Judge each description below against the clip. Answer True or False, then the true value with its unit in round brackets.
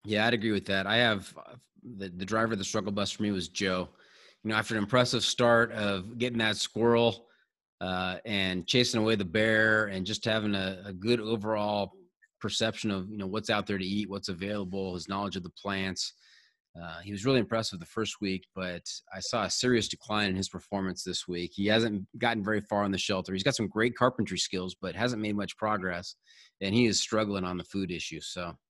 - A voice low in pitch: True (105 Hz)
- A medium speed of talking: False (220 wpm)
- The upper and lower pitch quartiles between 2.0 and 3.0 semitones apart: True (2.7 semitones)